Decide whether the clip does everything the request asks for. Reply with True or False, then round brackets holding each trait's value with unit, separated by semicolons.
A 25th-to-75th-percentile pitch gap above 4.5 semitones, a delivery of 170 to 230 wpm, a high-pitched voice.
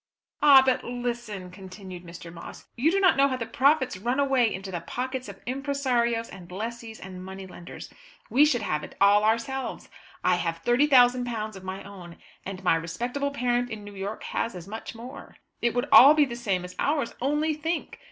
True (5.5 semitones; 190 wpm; 235 Hz)